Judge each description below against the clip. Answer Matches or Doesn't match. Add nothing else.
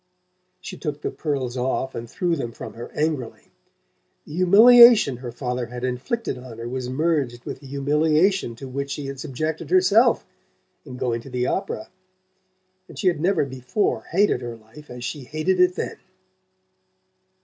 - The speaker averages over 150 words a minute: Matches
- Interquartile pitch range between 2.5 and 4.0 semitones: Doesn't match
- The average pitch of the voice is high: Doesn't match